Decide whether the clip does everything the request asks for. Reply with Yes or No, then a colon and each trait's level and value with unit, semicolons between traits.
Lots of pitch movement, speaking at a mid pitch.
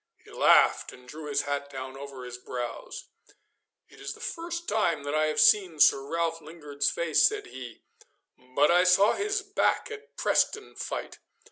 Yes: wide, 6.7 semitones; medium, 155 Hz